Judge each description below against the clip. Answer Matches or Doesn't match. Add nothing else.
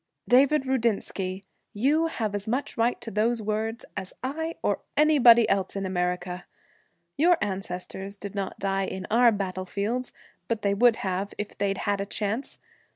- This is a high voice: Matches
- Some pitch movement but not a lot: Matches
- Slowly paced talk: Doesn't match